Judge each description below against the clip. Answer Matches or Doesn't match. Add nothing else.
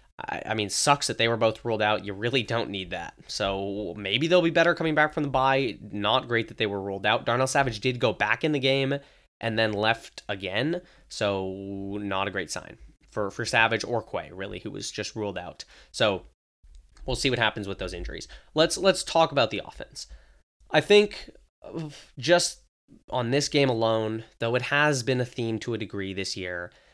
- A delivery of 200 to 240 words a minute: Matches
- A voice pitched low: Matches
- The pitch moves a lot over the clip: Matches